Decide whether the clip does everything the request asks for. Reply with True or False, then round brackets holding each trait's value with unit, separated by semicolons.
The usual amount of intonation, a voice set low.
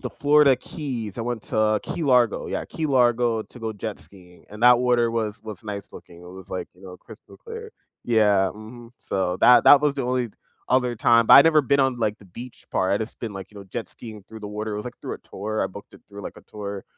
True (3.4 semitones; 110 Hz)